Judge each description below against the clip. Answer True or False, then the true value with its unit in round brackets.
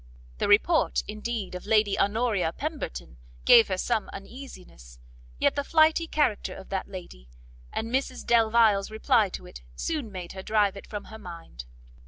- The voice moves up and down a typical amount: True (4.1 semitones)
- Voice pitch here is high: True (210 Hz)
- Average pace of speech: True (160 wpm)